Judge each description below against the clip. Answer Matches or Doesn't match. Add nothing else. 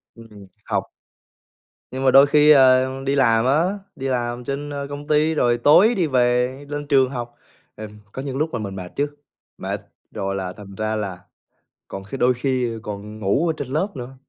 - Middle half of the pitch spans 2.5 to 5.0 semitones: Matches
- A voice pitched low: Matches